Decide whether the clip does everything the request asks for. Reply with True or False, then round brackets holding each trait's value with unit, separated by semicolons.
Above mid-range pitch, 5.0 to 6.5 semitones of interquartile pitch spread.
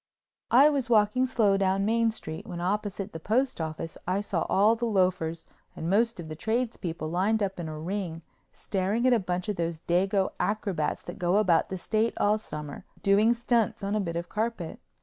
False (195 Hz; 4.2 semitones)